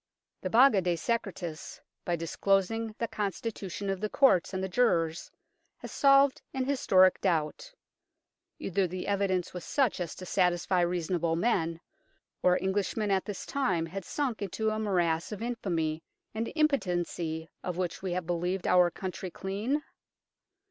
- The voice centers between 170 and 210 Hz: Yes, high, 190 Hz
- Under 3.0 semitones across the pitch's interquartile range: No, average, 3.8 semitones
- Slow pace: No, average, 150 wpm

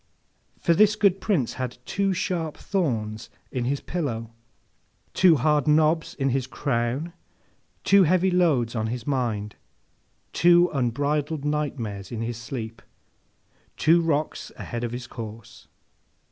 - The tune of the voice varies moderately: No, wide, 6.0 semitones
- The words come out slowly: Yes, slow, 130 wpm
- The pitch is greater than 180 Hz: No, medium, 140 Hz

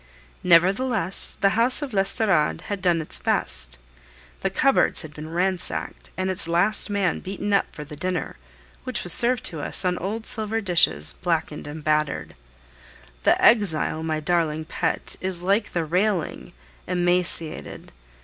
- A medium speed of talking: Yes, average, 150 wpm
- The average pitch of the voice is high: No, medium, 180 Hz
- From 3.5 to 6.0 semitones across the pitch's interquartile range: Yes, average, 3.9 semitones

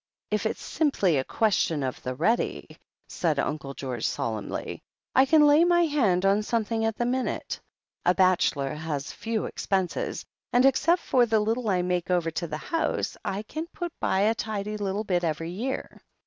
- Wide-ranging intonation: Yes, wide, 6.6 semitones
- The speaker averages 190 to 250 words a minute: No, average, 175 wpm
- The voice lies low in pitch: No, high, 200 Hz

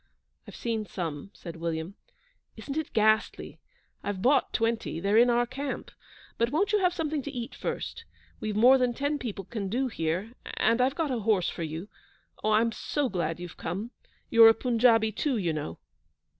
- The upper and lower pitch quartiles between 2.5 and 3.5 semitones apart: No, average, 5.0 semitones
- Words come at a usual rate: Yes, average, 185 wpm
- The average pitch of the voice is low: No, high, 225 Hz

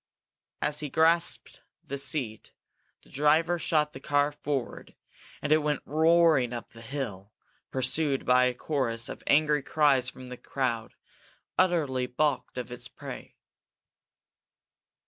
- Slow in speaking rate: Yes, slow, 130 wpm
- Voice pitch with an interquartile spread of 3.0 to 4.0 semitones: Yes, average, 3.4 semitones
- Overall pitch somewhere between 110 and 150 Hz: Yes, medium, 140 Hz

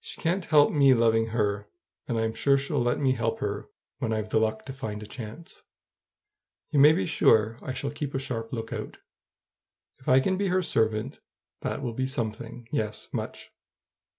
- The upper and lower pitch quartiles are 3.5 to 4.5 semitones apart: Yes, average, 3.9 semitones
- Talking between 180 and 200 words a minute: Yes, average, 185 wpm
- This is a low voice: Yes, low, 120 Hz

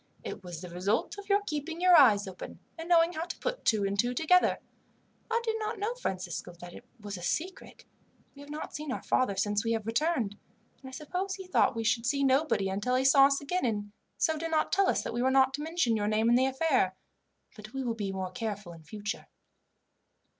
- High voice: Yes, very high, 260 Hz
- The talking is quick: Yes, fast, 225 wpm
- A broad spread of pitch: Yes, wide, 7.9 semitones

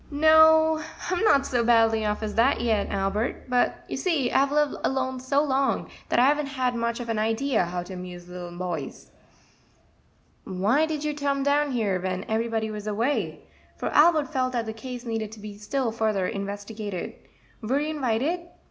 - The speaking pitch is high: Yes, high, 235 Hz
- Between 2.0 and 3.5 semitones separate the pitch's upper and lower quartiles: No, average, 5.1 semitones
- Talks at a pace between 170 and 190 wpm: Yes, average, 175 wpm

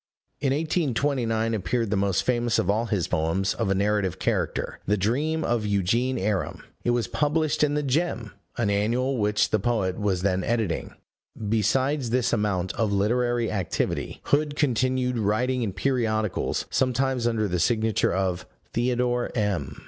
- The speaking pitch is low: Yes, low, 115 Hz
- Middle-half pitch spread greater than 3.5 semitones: Yes, average, 3.9 semitones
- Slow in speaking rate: No, average, 155 wpm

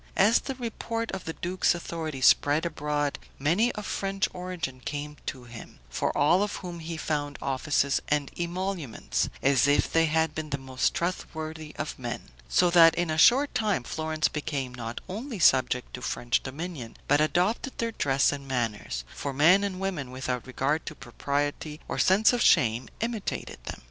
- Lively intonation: No, average, 5.0 semitones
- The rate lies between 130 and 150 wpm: No, average, 175 wpm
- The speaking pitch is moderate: Yes, medium, 155 Hz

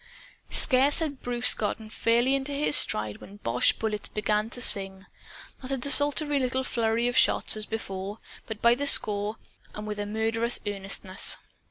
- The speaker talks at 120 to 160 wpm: No, average, 170 wpm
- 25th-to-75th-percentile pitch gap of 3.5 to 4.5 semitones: Yes, average, 3.9 semitones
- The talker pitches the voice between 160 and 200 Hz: No, high, 225 Hz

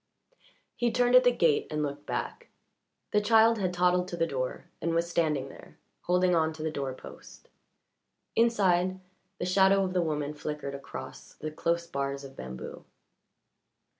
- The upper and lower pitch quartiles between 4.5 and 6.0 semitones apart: No, average, 4.1 semitones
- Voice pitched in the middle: Yes, medium, 170 Hz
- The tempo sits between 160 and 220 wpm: Yes, average, 165 wpm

